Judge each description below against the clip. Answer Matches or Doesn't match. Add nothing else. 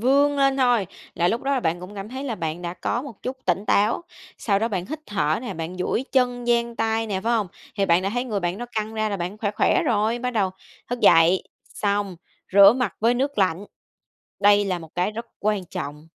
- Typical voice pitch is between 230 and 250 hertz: Doesn't match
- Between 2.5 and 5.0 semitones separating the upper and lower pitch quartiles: Matches